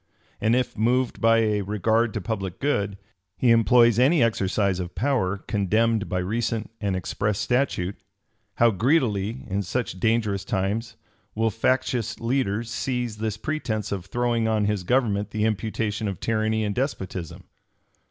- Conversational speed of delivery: Yes, average, 145 wpm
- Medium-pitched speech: No, low, 110 Hz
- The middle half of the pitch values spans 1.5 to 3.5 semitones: Yes, average, 2.8 semitones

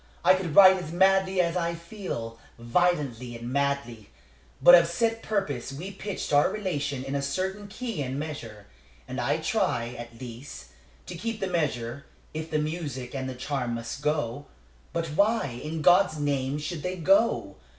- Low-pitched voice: No, medium, 150 Hz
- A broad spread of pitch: Yes, wide, 6.0 semitones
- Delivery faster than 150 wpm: Yes, average, 170 wpm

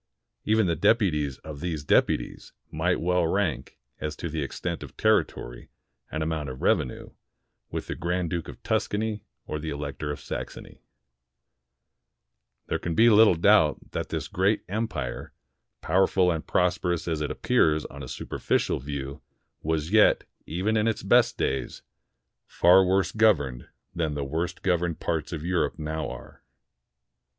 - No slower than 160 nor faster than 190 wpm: No, average, 150 wpm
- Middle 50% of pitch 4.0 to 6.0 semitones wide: No, average, 3.6 semitones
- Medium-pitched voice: No, very low, 85 Hz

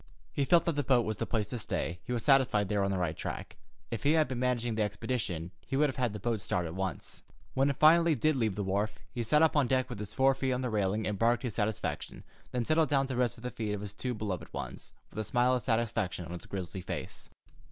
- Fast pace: Yes, fast, 270 wpm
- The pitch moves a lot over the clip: No, average, 4.2 semitones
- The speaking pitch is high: No, low, 115 Hz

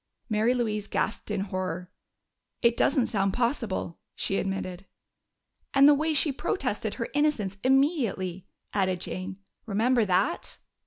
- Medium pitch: No, high, 215 Hz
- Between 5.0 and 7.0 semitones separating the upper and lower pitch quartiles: Yes, wide, 5.4 semitones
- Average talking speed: No, slow, 125 wpm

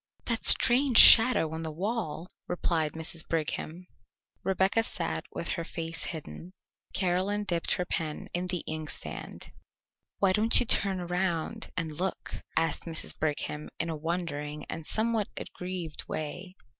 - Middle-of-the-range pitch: Yes, medium, 175 Hz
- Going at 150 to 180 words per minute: No, average, 140 wpm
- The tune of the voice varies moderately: Yes, average, 3.2 semitones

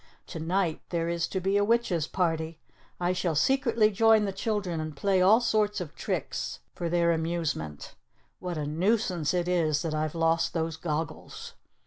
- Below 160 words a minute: No, average, 170 wpm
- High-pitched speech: No, medium, 170 Hz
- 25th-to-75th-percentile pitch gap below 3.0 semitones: No, average, 3.5 semitones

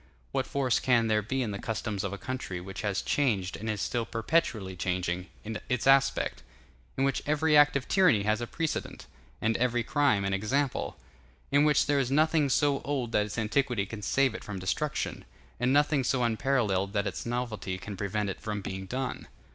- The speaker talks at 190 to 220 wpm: Yes, average, 195 wpm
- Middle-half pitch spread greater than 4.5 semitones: Yes, average, 5.2 semitones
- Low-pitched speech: Yes, low, 115 Hz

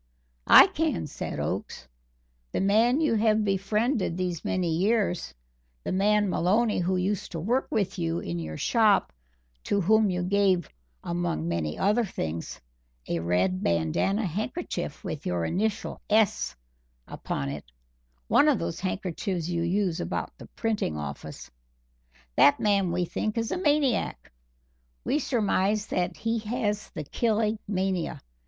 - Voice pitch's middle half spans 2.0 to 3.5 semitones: No, average, 4.5 semitones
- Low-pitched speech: No, high, 195 Hz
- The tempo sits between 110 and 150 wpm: Yes, average, 140 wpm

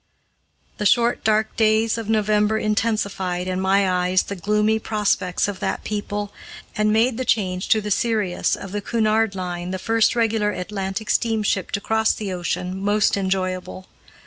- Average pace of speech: Yes, average, 160 wpm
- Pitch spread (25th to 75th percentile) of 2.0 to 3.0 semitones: Yes, narrow, 2.6 semitones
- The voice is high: Yes, high, 210 Hz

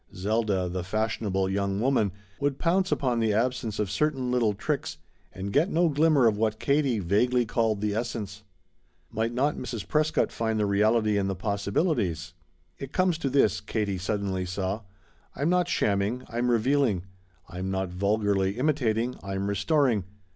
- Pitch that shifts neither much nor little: Yes, average, 4.4 semitones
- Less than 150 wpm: No, average, 155 wpm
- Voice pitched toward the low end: Yes, low, 110 Hz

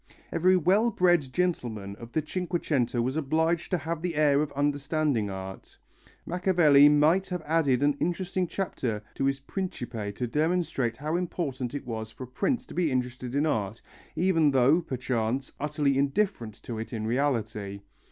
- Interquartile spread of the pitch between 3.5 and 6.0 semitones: Yes, wide, 5.5 semitones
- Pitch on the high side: No, medium, 145 Hz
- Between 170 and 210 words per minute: No, average, 160 wpm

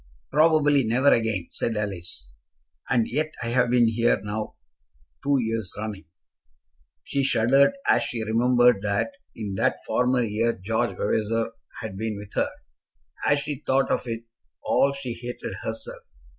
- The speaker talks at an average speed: Yes, average, 145 wpm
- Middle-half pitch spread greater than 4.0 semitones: No, average, 3.1 semitones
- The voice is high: No, low, 115 Hz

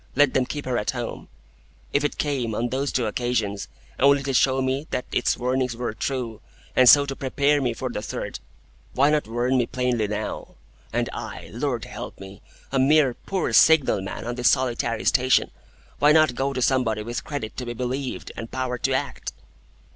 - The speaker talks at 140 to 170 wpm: No, average, 190 wpm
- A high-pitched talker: No, low, 130 Hz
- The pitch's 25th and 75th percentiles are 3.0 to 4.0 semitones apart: No, narrow, 2.5 semitones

